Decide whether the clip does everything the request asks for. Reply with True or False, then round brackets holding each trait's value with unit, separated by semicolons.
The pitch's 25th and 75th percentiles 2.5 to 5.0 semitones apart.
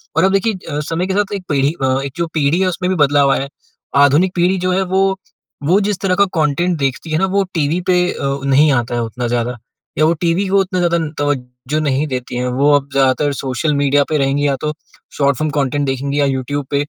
True (4.5 semitones)